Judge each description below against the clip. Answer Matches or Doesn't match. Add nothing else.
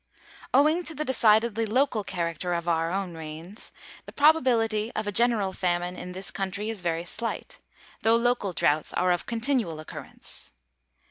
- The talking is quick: Doesn't match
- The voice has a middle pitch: Doesn't match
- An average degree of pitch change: Matches